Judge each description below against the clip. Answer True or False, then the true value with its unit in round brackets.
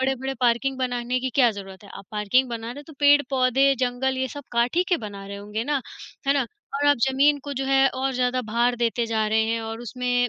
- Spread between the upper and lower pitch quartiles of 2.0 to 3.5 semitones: True (2.9 semitones)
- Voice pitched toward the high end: True (250 Hz)